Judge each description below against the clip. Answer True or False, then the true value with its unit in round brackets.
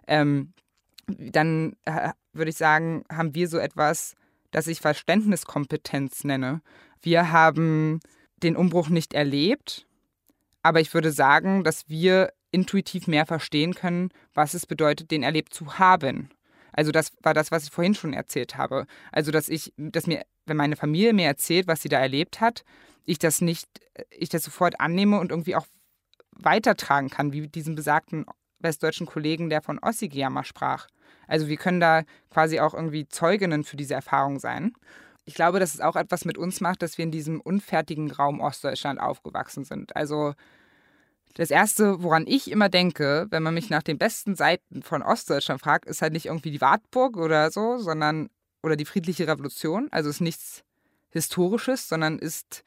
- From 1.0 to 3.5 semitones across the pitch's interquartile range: True (2.7 semitones)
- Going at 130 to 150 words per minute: False (170 wpm)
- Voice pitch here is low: False (160 Hz)